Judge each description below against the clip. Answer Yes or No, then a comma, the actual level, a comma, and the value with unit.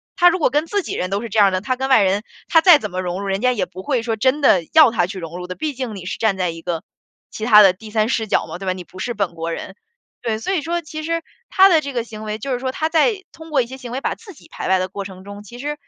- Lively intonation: Yes, wide, 7.2 semitones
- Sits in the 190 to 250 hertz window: Yes, high, 225 Hz